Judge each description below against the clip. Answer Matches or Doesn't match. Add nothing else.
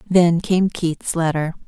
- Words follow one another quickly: Doesn't match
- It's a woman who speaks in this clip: Matches